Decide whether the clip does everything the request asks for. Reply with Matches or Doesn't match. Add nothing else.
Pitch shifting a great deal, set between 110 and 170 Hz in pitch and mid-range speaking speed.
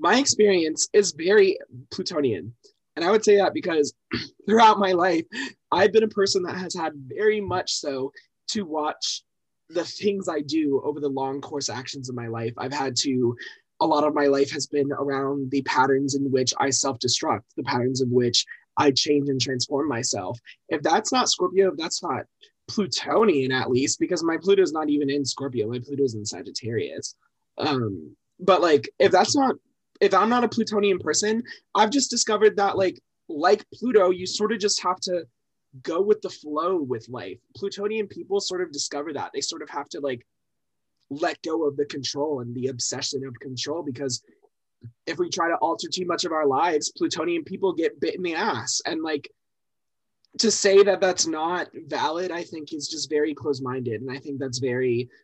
Matches